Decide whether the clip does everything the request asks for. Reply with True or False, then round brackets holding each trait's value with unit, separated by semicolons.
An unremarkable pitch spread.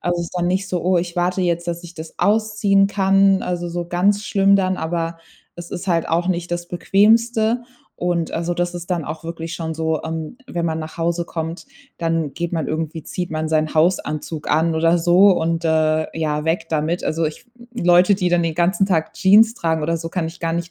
False (2.1 semitones)